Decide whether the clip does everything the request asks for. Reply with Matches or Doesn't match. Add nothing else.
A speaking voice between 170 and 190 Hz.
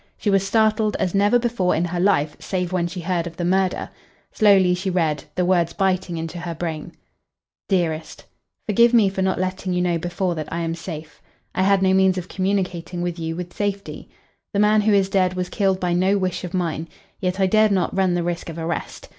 Matches